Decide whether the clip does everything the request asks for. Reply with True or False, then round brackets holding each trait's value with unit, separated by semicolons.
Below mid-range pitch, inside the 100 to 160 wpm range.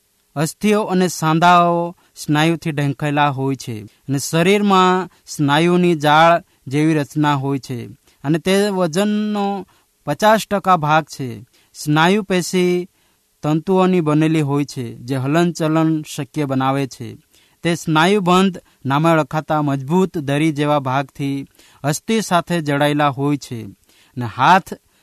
False (155 Hz; 115 wpm)